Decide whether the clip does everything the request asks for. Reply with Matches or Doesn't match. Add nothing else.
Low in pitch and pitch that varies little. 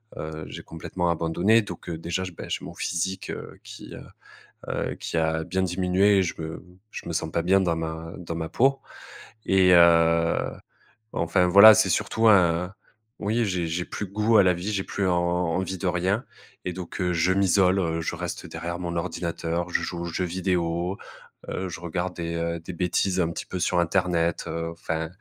Matches